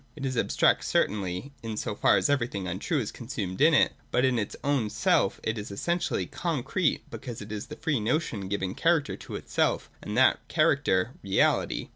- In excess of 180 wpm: Yes, average, 190 wpm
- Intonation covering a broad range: Yes, wide, 5.9 semitones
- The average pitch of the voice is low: Yes, low, 115 Hz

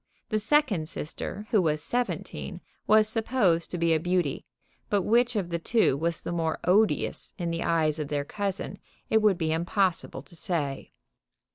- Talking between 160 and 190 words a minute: Yes, average, 170 wpm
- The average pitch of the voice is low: No, medium, 175 Hz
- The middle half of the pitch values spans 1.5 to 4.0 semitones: No, average, 4.8 semitones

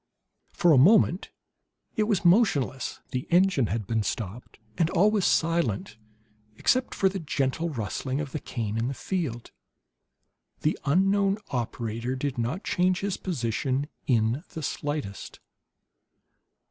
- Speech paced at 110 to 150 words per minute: Yes, slow, 135 wpm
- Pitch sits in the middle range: Yes, medium, 145 Hz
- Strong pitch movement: Yes, wide, 7.4 semitones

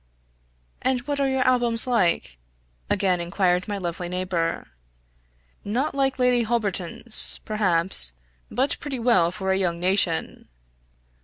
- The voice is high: Yes, high, 200 Hz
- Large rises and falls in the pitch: Yes, wide, 5.7 semitones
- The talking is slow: Yes, slow, 125 wpm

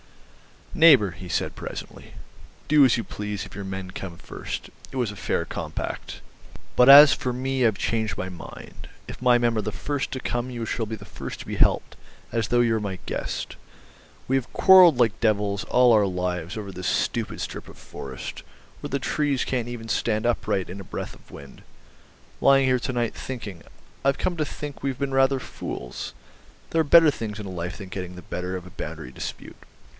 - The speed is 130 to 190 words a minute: No, average, 200 wpm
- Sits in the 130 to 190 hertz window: No, low, 115 Hz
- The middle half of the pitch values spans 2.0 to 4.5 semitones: No, average, 5.3 semitones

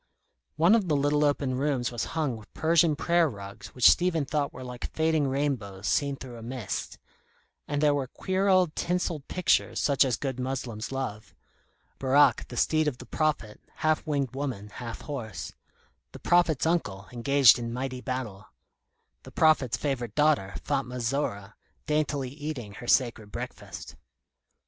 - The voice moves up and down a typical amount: Yes, average, 4.0 semitones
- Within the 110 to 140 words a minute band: No, average, 155 wpm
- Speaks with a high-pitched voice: No, low, 135 Hz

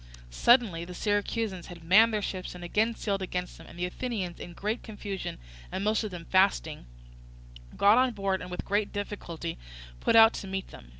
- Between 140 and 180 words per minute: No, average, 190 wpm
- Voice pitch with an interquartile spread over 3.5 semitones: No, average, 3.2 semitones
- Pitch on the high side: Yes, high, 195 Hz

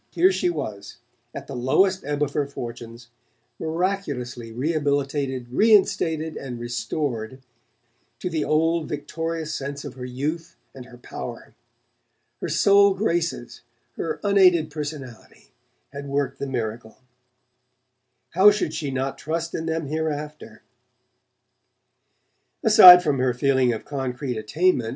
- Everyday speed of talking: No, slow, 125 wpm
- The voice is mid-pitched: Yes, medium, 145 Hz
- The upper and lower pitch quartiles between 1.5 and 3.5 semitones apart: No, average, 4.5 semitones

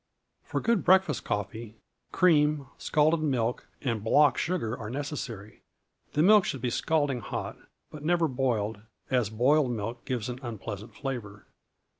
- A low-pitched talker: Yes, low, 130 Hz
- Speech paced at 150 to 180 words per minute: No, average, 140 wpm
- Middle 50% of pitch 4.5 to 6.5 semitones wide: Yes, average, 5.1 semitones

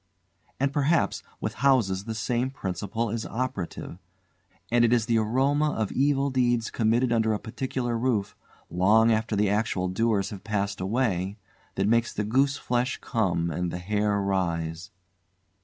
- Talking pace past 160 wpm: No, average, 150 wpm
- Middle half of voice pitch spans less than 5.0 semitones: Yes, average, 3.9 semitones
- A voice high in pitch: No, low, 110 Hz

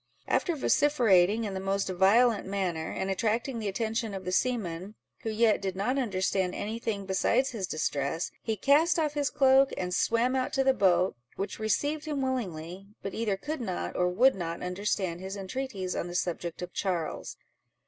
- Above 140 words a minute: Yes, average, 180 wpm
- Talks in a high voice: Yes, high, 200 Hz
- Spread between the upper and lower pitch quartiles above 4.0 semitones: Yes, average, 5.2 semitones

